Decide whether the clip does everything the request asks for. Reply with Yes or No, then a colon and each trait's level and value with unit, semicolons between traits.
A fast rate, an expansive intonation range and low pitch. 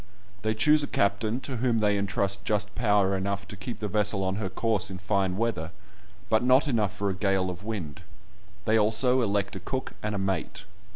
No: fast, 210 wpm; narrow, 2.5 semitones; low, 105 Hz